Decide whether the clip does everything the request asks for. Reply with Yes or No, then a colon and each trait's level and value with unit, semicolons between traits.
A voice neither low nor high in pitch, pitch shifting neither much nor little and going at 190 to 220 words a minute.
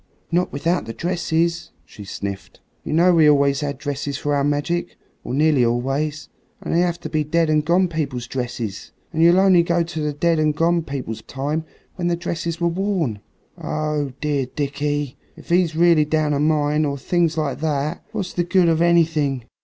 Yes: medium, 155 Hz; average, 3.1 semitones; average, 195 wpm